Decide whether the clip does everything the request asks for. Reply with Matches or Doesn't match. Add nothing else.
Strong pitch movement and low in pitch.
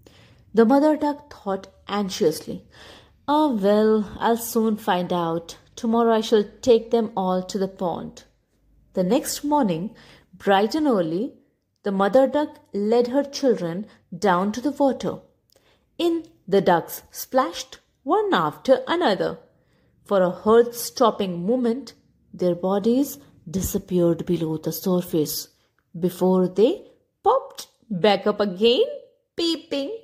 Doesn't match